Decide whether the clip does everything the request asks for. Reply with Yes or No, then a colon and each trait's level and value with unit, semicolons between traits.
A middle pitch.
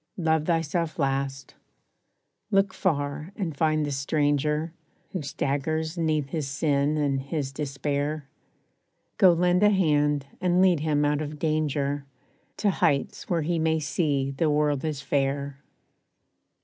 Yes: medium, 150 Hz